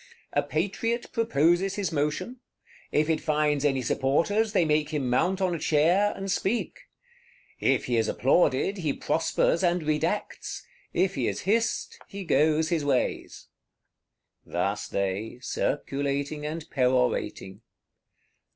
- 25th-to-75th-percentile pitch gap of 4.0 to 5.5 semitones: Yes, average, 5.2 semitones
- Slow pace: Yes, slow, 130 wpm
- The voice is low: No, medium, 155 Hz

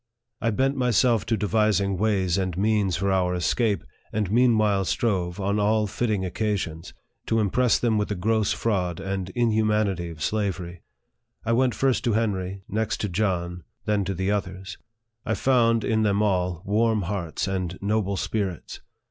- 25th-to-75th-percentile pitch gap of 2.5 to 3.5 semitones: Yes, average, 2.9 semitones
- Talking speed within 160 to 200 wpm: Yes, average, 165 wpm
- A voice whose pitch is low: Yes, low, 105 Hz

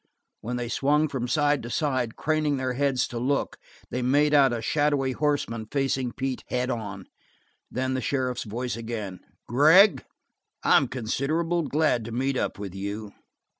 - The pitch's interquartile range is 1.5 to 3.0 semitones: No, average, 3.5 semitones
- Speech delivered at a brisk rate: No, average, 160 wpm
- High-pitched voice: No, low, 130 Hz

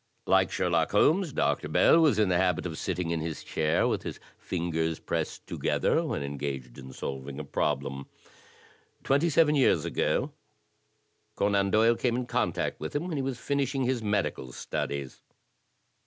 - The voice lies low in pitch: Yes, very low, 95 Hz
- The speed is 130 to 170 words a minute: Yes, average, 165 wpm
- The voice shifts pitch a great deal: Yes, wide, 8.9 semitones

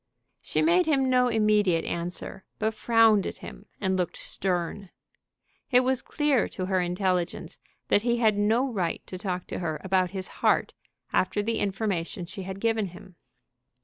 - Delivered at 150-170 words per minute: Yes, average, 165 wpm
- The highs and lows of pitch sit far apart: No, average, 3.7 semitones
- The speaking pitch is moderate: No, high, 200 Hz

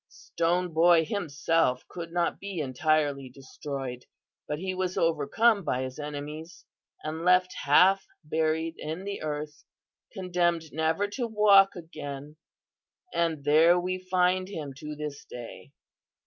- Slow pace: Yes, slow, 130 wpm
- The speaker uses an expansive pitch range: No, average, 3.5 semitones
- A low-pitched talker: No, medium, 160 Hz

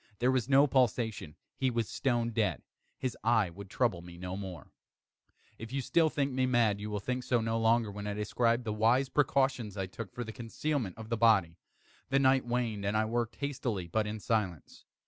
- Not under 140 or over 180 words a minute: No, fast, 205 wpm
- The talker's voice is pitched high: No, low, 115 Hz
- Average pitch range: Yes, average, 3.5 semitones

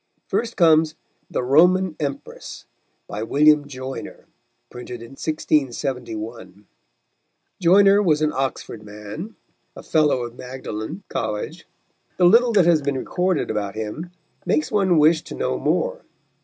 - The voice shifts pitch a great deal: Yes, wide, 6.3 semitones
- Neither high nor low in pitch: Yes, medium, 150 Hz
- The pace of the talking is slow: Yes, slow, 130 wpm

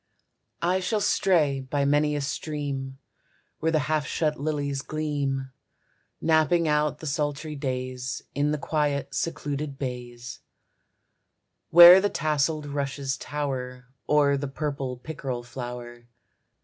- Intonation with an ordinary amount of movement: No, narrow, 2.3 semitones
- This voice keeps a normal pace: No, slow, 120 wpm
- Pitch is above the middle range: No, medium, 145 Hz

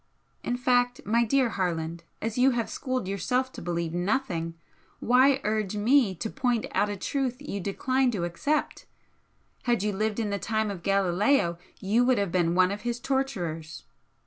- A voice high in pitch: Yes, high, 215 Hz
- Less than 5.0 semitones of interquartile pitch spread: No, average, 5.3 semitones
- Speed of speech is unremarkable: Yes, average, 170 wpm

